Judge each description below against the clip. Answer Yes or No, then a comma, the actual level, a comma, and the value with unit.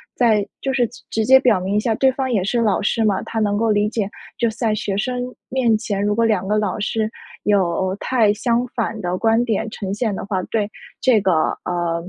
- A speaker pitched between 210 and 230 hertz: Yes, high, 215 Hz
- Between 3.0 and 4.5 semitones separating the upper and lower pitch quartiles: No, narrow, 2.5 semitones